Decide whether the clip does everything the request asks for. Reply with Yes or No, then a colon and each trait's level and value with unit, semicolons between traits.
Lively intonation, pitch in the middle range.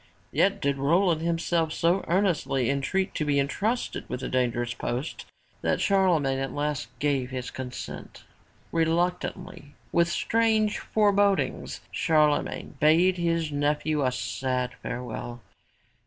No: average, 4.9 semitones; medium, 155 Hz